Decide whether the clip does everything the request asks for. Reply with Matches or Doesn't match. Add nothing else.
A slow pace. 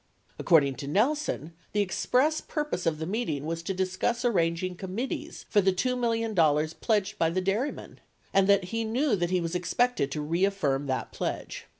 Doesn't match